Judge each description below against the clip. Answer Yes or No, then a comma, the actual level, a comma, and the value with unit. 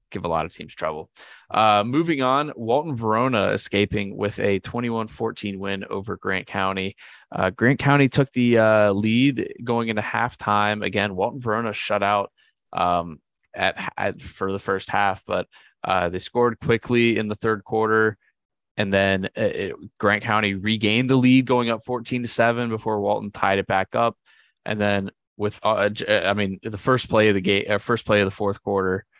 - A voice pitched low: Yes, low, 105 Hz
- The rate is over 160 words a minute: Yes, average, 185 wpm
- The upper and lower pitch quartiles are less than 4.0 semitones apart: Yes, average, 2.8 semitones